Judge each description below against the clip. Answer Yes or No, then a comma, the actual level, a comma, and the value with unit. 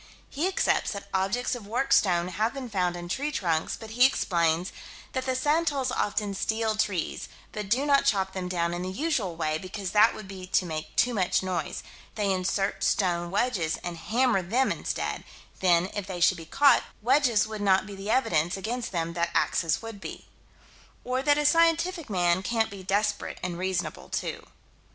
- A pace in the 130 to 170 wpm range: No, average, 190 wpm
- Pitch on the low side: No, high, 200 Hz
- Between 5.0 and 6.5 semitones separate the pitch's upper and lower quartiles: Yes, wide, 5.4 semitones